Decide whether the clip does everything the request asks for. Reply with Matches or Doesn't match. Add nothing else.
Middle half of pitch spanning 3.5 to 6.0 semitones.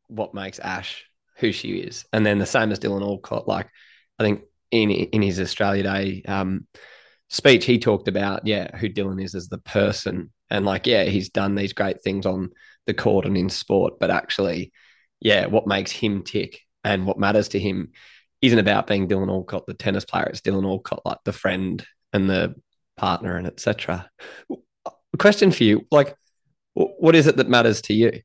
Doesn't match